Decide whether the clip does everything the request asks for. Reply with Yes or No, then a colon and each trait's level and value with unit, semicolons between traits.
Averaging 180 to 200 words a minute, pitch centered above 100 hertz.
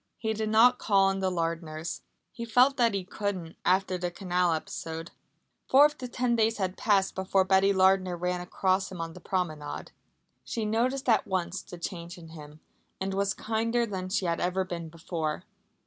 Yes: average, 185 wpm; high, 190 Hz